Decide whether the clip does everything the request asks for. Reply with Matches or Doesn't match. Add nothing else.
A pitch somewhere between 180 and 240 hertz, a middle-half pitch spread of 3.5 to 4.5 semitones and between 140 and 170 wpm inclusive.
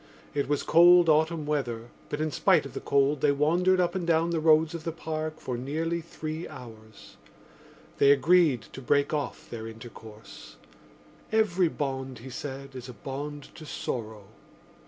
Doesn't match